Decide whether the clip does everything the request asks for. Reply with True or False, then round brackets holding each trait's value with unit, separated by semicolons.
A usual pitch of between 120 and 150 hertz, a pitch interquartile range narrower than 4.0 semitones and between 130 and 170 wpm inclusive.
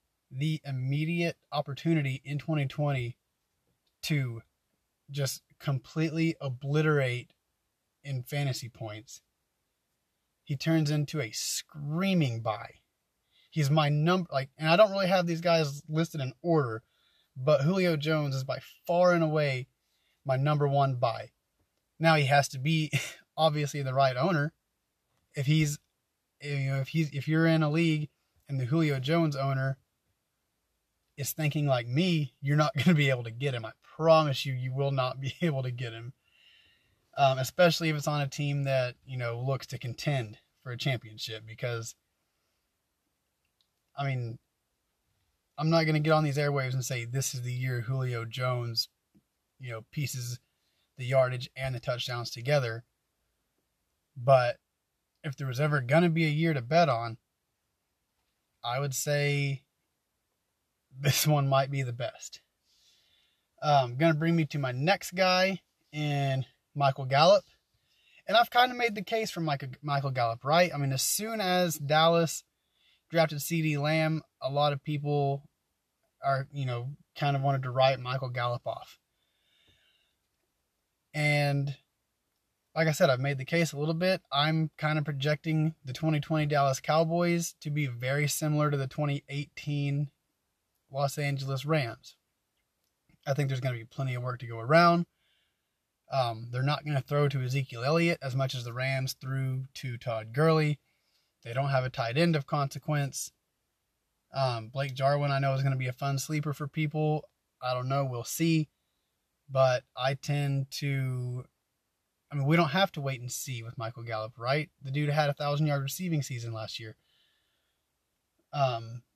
True (140 Hz; 3.1 semitones; 160 wpm)